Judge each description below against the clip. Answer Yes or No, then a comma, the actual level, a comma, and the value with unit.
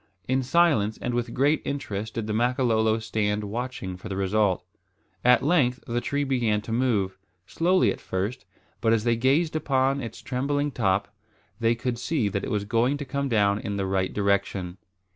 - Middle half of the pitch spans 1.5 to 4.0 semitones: No, average, 4.4 semitones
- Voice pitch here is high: No, low, 115 Hz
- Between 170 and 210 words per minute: Yes, average, 180 wpm